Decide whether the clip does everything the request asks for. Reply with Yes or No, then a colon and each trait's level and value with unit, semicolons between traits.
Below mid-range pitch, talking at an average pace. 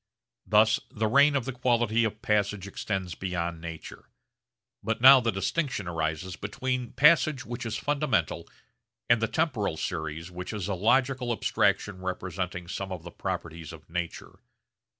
Yes: low, 105 Hz; average, 150 wpm